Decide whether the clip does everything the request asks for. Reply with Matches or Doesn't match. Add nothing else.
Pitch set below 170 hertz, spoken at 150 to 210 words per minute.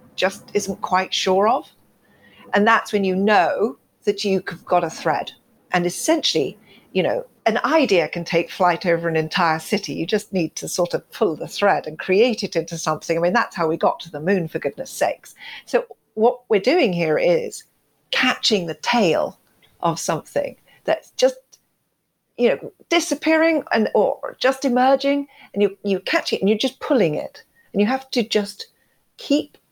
Doesn't match